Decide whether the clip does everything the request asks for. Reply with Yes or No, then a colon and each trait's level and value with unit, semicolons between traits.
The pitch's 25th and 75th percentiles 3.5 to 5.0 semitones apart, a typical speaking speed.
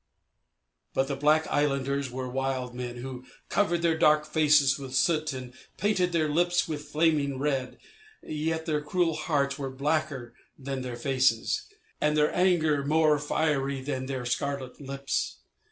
No: average, 2.8 semitones; average, 150 wpm